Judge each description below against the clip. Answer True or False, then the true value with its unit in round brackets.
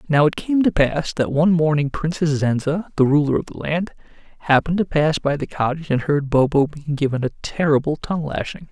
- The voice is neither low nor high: True (150 Hz)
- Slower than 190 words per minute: False (205 wpm)